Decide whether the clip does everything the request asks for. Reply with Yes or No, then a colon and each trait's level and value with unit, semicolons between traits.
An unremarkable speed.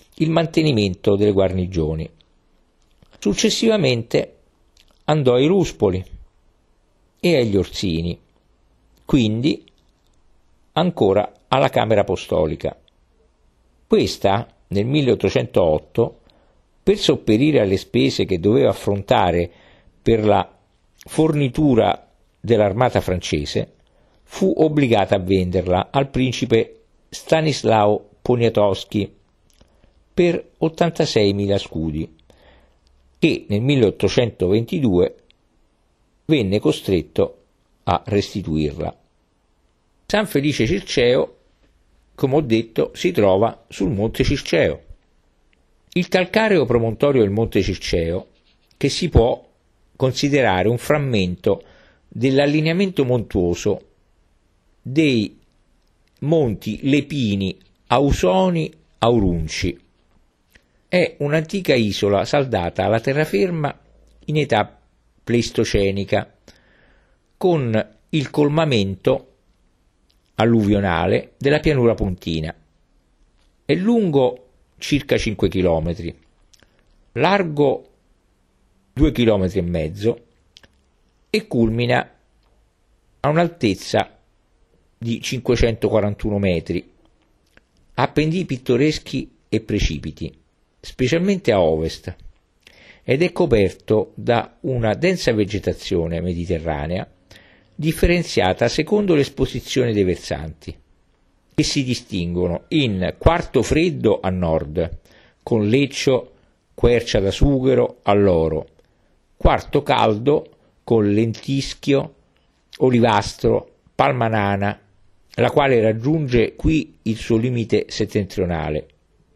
No: slow, 80 wpm